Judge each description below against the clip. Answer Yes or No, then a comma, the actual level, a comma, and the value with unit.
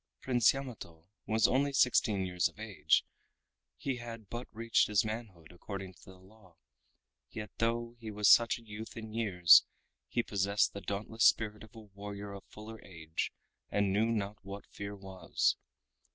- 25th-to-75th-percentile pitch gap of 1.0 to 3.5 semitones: Yes, average, 2.8 semitones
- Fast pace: No, average, 165 wpm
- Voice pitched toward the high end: No, low, 105 Hz